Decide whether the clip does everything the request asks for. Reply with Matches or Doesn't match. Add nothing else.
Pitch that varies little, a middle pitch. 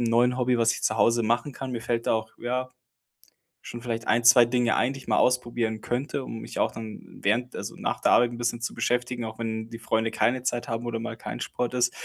Doesn't match